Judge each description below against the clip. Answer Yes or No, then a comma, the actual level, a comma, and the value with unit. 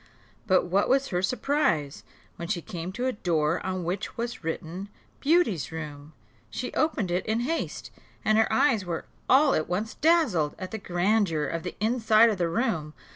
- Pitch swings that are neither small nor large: No, wide, 5.8 semitones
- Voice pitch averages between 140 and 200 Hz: Yes, high, 190 Hz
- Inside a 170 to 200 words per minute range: Yes, average, 180 wpm